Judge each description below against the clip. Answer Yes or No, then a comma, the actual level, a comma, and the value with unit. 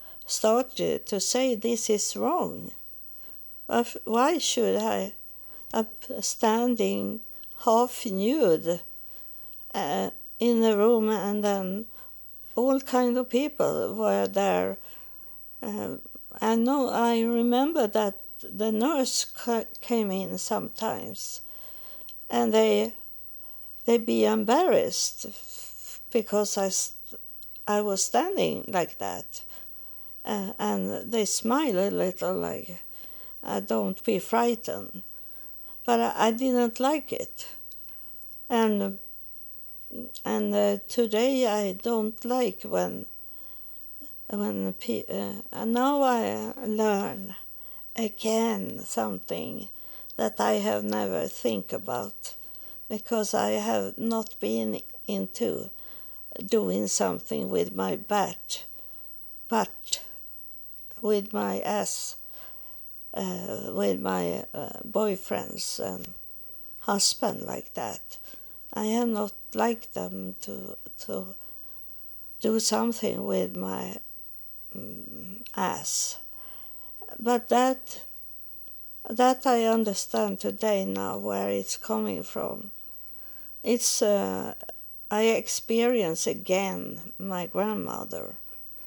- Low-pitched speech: No, high, 220 Hz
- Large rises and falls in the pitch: No, average, 4.0 semitones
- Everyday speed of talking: No, slow, 95 wpm